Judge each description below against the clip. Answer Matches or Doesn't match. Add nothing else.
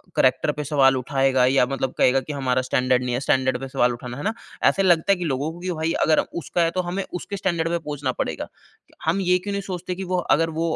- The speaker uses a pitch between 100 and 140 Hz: Doesn't match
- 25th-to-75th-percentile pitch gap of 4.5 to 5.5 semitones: Matches